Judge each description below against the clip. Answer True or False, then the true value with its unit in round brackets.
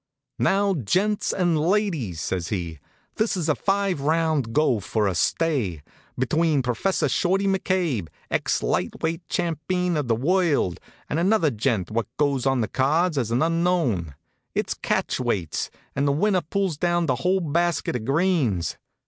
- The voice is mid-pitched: True (155 Hz)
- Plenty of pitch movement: True (7.0 semitones)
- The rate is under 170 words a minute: True (155 wpm)